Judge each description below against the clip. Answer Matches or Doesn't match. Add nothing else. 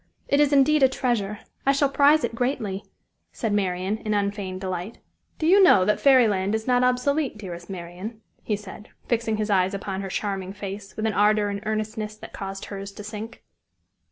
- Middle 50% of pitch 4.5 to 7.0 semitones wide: Doesn't match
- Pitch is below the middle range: Doesn't match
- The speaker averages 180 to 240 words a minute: Matches